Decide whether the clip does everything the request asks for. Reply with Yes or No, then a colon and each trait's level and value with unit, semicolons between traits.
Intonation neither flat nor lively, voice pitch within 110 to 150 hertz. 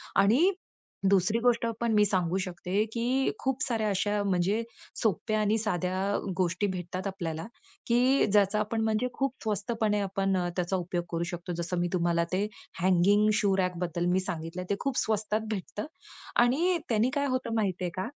No: average, 3.7 semitones; high, 200 Hz